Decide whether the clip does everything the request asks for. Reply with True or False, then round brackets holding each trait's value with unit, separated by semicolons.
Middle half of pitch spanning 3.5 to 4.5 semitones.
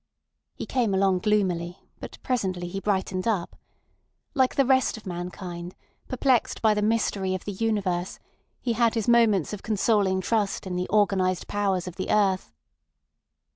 False (3.1 semitones)